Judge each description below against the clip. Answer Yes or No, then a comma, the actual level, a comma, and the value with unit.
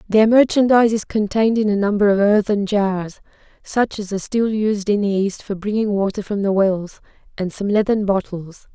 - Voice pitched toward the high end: Yes, high, 205 Hz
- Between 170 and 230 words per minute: Yes, average, 190 wpm